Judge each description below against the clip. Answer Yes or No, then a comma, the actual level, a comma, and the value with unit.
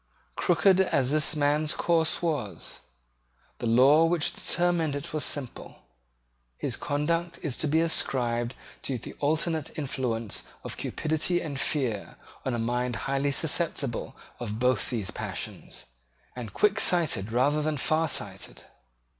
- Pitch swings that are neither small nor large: Yes, average, 4.6 semitones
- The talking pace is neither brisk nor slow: No, slow, 130 wpm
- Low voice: No, medium, 145 Hz